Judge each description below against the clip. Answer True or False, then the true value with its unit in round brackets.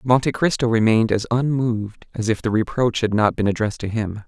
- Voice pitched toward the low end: True (115 Hz)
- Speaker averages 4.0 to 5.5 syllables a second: False (5.9 syllables/s)